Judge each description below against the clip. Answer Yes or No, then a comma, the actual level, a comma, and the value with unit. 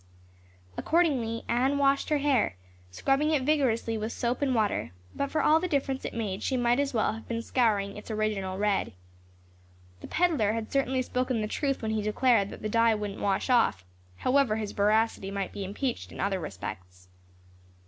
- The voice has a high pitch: Yes, high, 230 Hz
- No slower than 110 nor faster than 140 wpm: No, average, 180 wpm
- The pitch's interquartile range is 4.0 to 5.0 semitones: Yes, average, 4.7 semitones